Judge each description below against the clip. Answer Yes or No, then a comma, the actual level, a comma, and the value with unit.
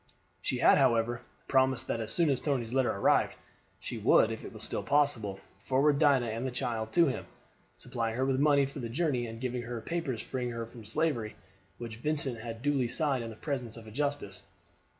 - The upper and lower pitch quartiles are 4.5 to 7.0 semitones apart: No, average, 3.5 semitones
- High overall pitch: No, low, 125 Hz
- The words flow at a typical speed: No, fast, 210 wpm